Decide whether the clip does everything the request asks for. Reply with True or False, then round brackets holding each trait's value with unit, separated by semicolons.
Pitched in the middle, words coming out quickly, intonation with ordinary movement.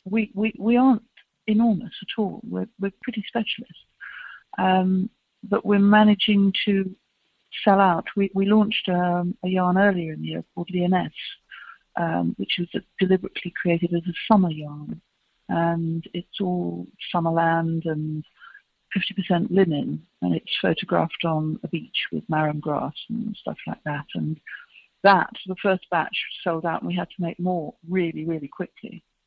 False (180 Hz; 160 wpm; 3.6 semitones)